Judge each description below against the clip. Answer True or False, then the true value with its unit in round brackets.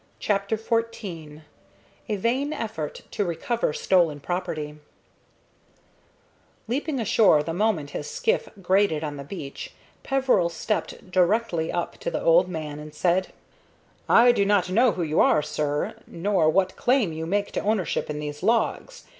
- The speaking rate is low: False (145 wpm)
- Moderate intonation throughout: False (6.1 semitones)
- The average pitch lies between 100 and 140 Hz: False (185 Hz)